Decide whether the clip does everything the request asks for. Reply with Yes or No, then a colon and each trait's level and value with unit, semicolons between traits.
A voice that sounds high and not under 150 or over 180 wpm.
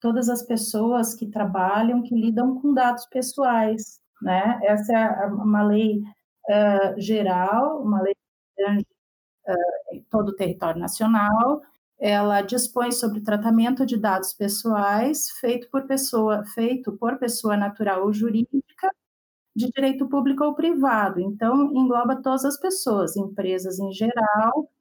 No: high, 225 Hz; average, 135 wpm